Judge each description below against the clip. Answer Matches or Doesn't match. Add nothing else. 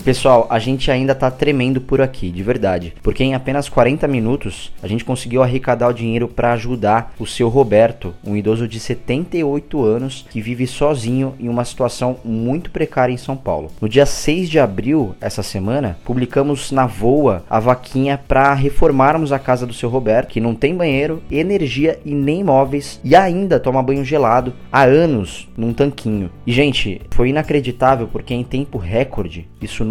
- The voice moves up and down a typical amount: Matches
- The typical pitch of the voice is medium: Doesn't match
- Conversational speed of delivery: Matches